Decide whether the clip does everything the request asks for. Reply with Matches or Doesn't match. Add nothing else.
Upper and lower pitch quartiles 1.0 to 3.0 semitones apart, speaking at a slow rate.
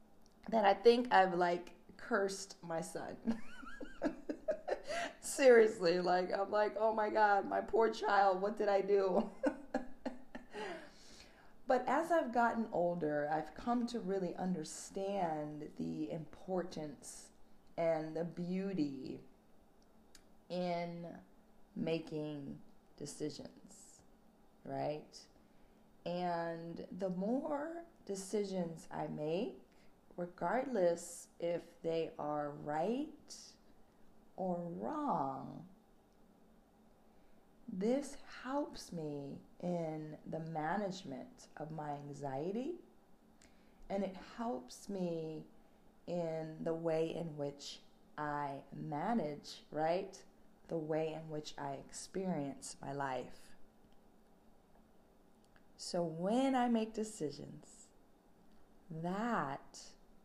Doesn't match